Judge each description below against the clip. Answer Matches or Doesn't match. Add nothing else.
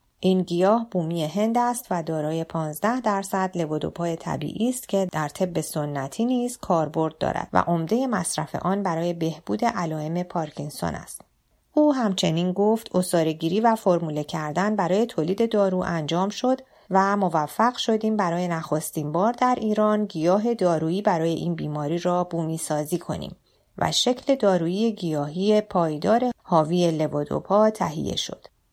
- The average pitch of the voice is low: Doesn't match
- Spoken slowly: Doesn't match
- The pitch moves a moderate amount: Matches